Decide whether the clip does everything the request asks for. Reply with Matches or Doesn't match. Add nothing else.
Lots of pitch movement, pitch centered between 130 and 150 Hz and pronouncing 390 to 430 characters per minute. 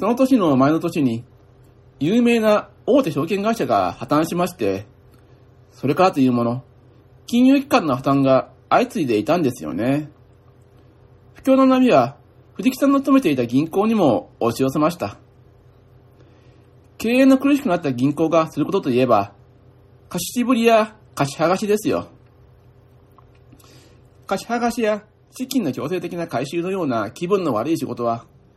Doesn't match